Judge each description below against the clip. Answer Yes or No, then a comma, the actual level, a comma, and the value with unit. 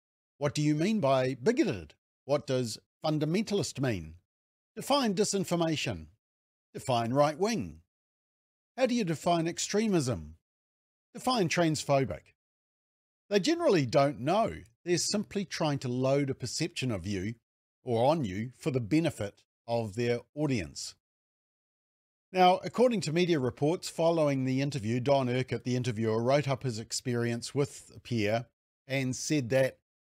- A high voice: No, low, 135 Hz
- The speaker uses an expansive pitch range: Yes, wide, 6.2 semitones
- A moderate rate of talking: No, slow, 130 wpm